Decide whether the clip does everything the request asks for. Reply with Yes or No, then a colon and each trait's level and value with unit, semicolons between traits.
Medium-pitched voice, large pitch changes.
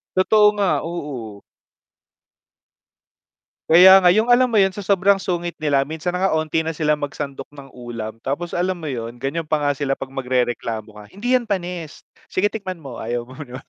Yes: medium, 155 Hz; wide, 5.8 semitones